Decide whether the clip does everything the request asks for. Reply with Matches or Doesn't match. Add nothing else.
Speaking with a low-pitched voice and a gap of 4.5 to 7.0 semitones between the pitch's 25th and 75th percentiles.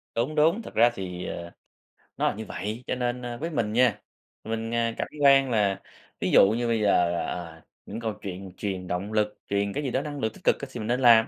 Doesn't match